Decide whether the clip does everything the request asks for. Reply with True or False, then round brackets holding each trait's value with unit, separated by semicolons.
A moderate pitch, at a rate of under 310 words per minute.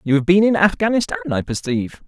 True (165 Hz; 200 wpm)